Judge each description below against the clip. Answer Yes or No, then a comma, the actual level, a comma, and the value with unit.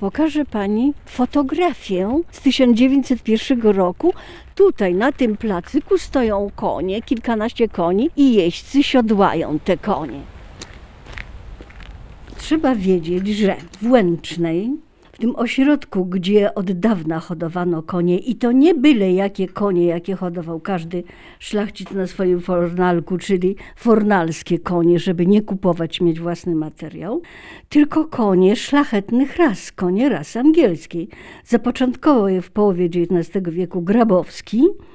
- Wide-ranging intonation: Yes, wide, 6.0 semitones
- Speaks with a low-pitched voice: No, high, 200 Hz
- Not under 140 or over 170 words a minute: No, average, 115 wpm